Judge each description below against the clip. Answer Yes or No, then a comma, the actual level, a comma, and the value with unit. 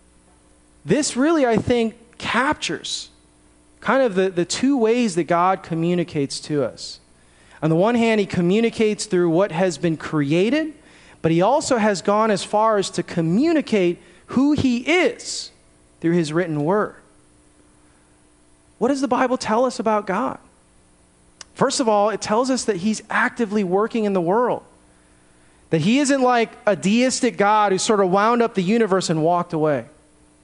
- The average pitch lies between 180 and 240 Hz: Yes, high, 190 Hz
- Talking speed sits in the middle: Yes, average, 160 wpm